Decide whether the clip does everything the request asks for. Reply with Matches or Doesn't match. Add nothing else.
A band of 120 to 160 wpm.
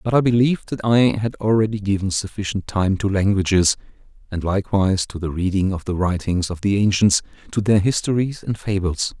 Doesn't match